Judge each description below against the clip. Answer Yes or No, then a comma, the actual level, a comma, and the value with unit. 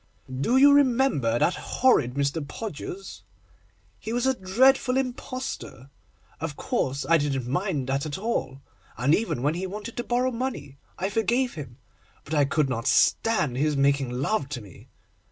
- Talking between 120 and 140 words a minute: No, average, 160 wpm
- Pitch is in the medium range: Yes, medium, 160 Hz